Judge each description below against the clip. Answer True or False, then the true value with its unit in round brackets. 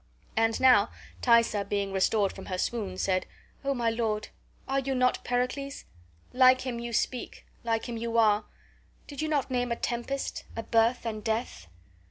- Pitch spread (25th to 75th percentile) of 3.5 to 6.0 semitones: False (2.8 semitones)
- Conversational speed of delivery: True (170 wpm)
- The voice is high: True (235 Hz)